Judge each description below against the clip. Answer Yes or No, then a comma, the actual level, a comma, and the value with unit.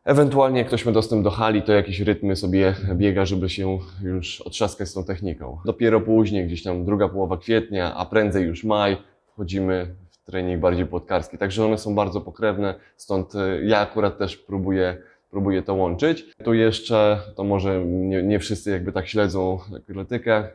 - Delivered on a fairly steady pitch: Yes, narrow, 2.2 semitones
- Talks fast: Yes, fast, 170 wpm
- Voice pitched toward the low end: Yes, low, 100 Hz